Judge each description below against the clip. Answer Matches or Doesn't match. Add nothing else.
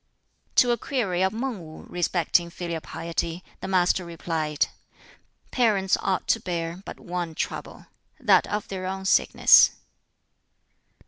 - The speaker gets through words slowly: Matches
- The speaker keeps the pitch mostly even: Matches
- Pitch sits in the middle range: Matches